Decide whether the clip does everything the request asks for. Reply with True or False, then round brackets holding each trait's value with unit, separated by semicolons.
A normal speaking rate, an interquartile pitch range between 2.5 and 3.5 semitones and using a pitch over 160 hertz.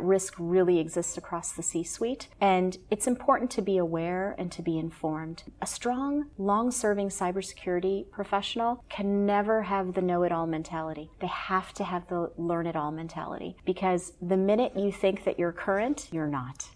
True (180 wpm; 3.0 semitones; 185 Hz)